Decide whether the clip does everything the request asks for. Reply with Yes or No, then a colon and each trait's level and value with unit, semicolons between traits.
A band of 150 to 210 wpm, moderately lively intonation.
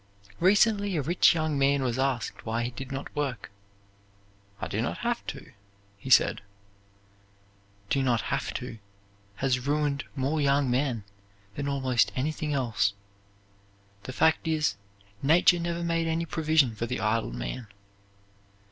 No: average, 140 wpm; average, 4.3 semitones